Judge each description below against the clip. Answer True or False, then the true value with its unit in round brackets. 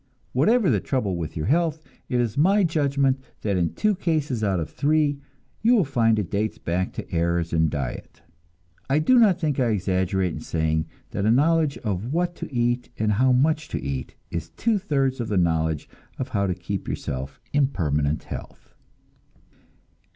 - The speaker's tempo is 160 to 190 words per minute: True (180 wpm)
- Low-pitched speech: True (120 Hz)